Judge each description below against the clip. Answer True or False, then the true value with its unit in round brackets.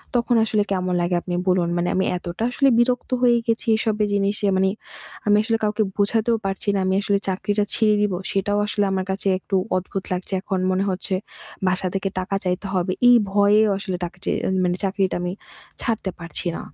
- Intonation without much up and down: True (2.3 semitones)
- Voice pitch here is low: False (195 Hz)